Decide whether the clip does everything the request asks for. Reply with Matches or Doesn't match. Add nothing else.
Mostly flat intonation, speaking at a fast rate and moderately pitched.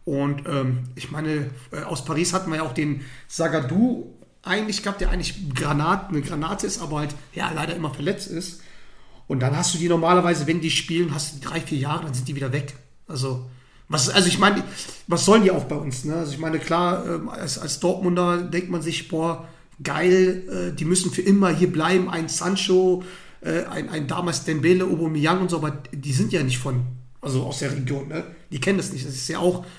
Doesn't match